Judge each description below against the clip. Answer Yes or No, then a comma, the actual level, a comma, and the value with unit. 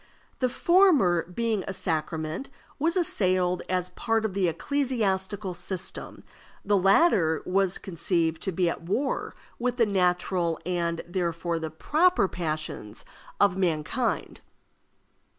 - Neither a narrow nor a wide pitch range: Yes, average, 4.9 semitones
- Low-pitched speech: No, medium, 185 Hz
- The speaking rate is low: Yes, slow, 120 wpm